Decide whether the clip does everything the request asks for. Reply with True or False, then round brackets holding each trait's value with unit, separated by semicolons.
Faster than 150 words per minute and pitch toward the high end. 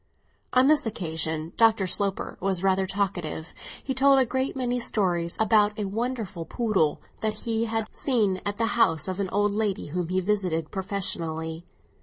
True (165 wpm; 200 Hz)